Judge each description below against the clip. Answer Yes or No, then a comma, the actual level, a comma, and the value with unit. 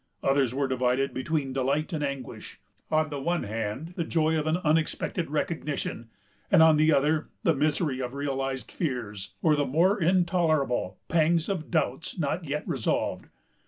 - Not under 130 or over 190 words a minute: Yes, average, 160 wpm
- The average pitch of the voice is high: No, medium, 150 Hz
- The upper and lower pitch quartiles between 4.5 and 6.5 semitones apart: No, average, 3.2 semitones